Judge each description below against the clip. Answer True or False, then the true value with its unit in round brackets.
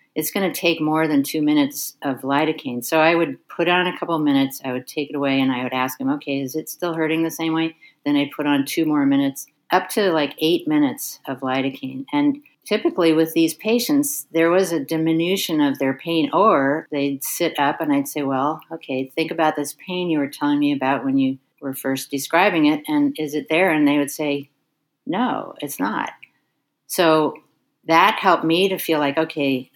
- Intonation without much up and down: False (3.2 semitones)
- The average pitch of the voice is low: False (155 Hz)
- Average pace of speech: False (215 wpm)